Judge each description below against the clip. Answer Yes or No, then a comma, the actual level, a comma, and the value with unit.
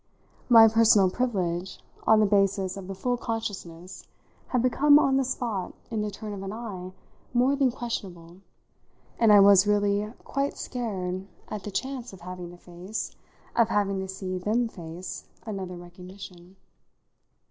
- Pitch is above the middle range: Yes, high, 200 Hz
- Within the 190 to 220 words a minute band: No, average, 155 wpm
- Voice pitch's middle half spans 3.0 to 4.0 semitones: Yes, average, 3.7 semitones